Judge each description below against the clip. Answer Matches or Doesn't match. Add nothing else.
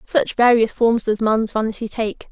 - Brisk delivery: Doesn't match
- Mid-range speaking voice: Doesn't match